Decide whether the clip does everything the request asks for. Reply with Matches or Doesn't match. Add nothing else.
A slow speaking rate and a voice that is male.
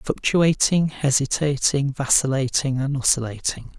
Matches